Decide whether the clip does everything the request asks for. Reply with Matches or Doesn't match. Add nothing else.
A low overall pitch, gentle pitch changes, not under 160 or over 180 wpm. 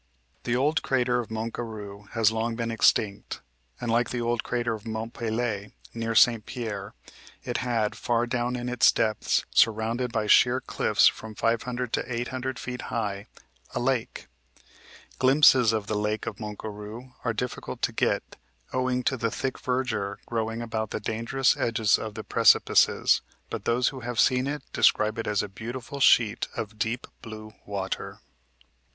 Matches